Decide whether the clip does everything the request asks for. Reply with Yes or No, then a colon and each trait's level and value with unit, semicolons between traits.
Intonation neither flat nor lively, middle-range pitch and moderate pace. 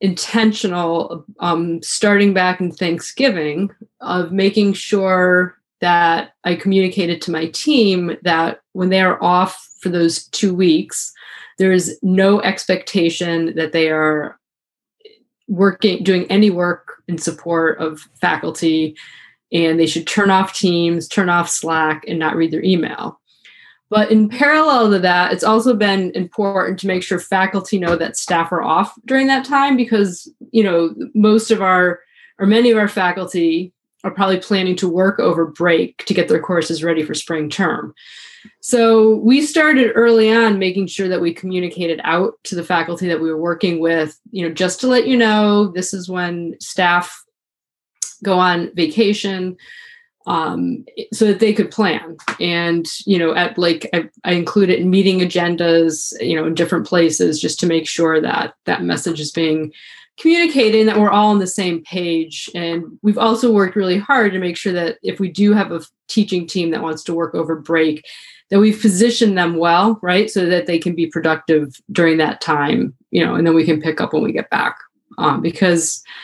Yes: average, 3.7 semitones; medium, 180 Hz; average, 175 wpm